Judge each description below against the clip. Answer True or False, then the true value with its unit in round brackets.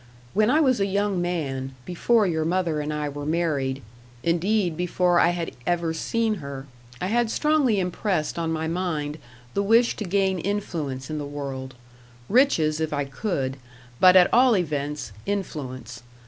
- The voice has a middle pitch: True (170 Hz)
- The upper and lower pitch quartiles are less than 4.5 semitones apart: False (5.3 semitones)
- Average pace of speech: True (160 wpm)